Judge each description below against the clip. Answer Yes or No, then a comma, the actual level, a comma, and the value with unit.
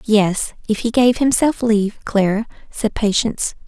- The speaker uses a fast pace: No, average, 145 wpm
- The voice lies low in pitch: No, high, 220 Hz